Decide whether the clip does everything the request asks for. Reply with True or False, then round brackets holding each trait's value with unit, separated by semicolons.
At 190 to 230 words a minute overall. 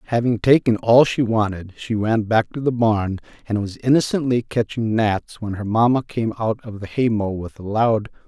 True (205 wpm)